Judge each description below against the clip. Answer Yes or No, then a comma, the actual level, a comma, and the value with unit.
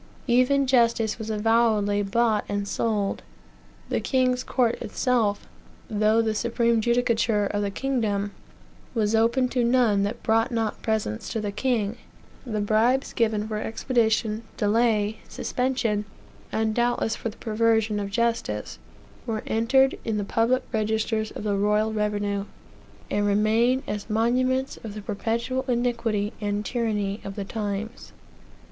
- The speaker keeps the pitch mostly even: Yes, narrow, 2.2 semitones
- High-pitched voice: Yes, high, 220 Hz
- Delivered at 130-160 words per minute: Yes, average, 140 wpm